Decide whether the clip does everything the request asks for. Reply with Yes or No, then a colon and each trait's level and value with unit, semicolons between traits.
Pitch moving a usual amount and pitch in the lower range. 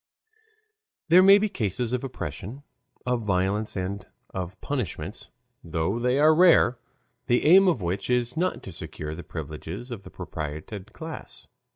No: wide, 7.6 semitones; low, 115 Hz